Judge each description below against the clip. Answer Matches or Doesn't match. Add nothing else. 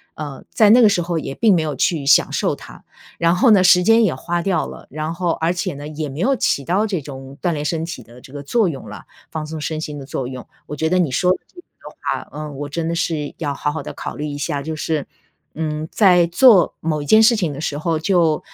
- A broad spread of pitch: Doesn't match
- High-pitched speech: Doesn't match